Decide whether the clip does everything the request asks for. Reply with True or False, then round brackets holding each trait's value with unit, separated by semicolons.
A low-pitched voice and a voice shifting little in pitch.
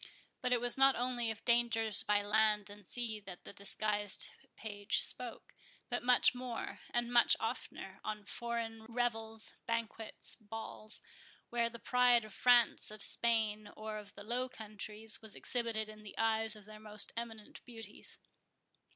False (225 Hz; 2.0 semitones)